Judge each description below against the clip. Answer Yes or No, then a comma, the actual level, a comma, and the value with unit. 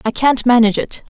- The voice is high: Yes, high, 240 Hz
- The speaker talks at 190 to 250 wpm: Yes, fast, 205 wpm